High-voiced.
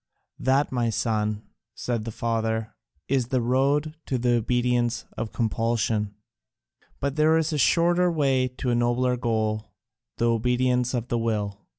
No: low, 120 Hz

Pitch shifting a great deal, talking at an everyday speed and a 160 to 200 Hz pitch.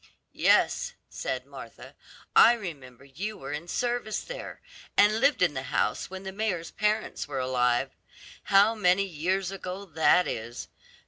Yes: wide, 6.4 semitones; average, 145 wpm; medium, 185 Hz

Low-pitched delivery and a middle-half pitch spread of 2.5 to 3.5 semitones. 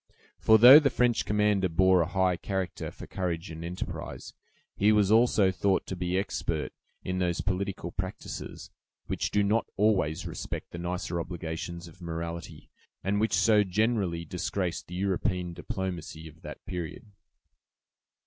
Yes: very low, 95 Hz; average, 3.0 semitones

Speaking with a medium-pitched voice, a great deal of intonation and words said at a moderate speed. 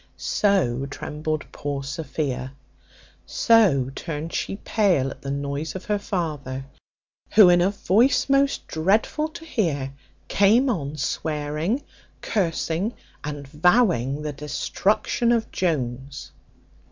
No: medium, 160 Hz; wide, 6.5 semitones; slow, 115 wpm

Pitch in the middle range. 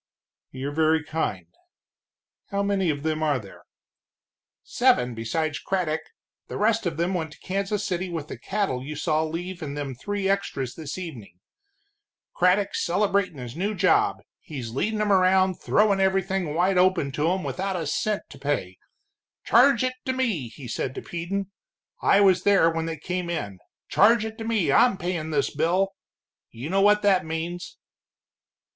Yes: medium, 175 Hz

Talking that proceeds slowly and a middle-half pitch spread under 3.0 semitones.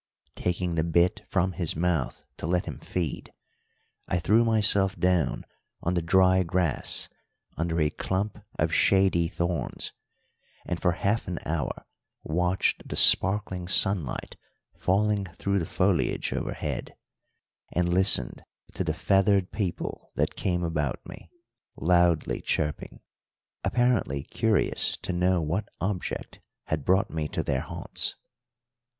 Yes: slow, 130 wpm; narrow, 2.6 semitones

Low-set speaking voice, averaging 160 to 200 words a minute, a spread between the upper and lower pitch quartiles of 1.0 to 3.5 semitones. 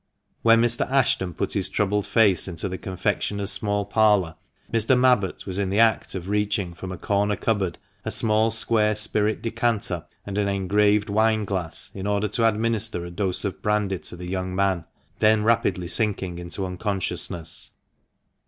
Yes: low, 100 Hz; average, 170 wpm; narrow, 2.6 semitones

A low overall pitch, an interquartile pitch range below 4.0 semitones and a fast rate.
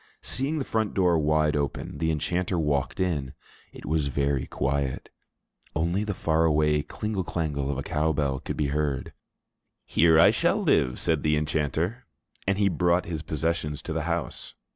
No: very low, 80 Hz; average, 3.1 semitones; average, 170 wpm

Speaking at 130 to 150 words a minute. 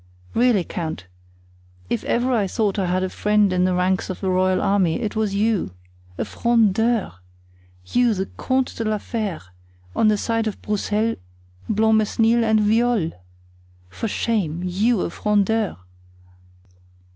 Yes: average, 145 wpm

